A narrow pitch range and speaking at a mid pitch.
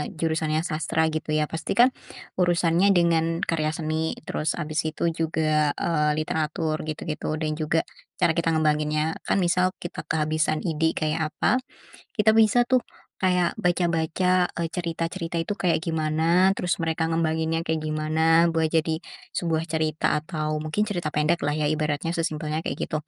Yes: narrow, 1.6 semitones; medium, 160 Hz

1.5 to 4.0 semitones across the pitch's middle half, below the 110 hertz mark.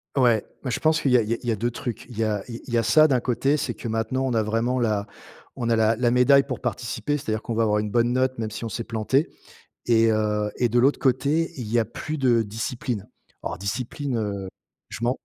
No: average, 2.7 semitones; low, 120 Hz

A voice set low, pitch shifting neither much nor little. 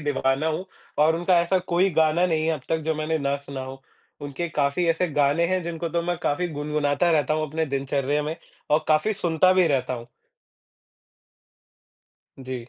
No: medium, 155 Hz; average, 3.1 semitones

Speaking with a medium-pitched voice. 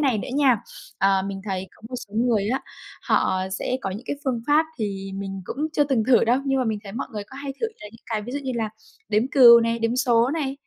No: high, 230 Hz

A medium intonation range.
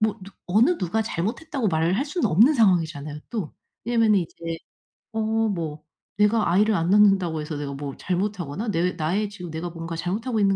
Yes: average, 4.7 semitones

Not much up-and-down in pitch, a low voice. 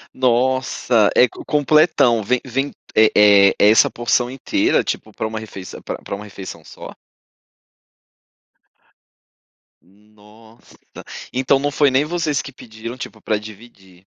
No: average, 3.8 semitones; low, 115 Hz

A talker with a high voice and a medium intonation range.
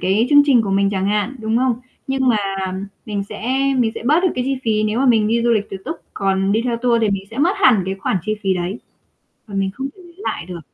Yes: high, 220 Hz; average, 4.4 semitones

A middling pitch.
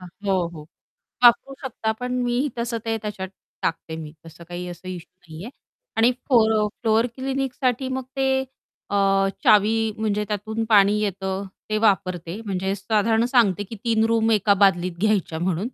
No: high, 210 Hz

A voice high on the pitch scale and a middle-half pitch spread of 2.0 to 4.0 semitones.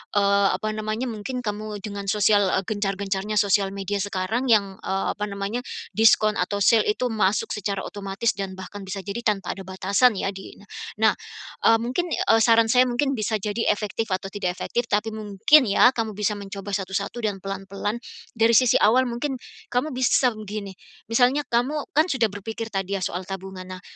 Yes: high, 210 Hz; narrow, 2.5 semitones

